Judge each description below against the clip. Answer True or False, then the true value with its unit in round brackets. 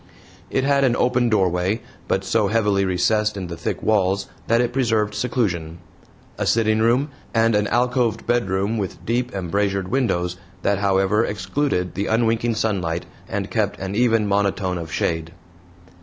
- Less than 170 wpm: True (155 wpm)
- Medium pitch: False (105 Hz)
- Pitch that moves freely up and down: False (3.5 semitones)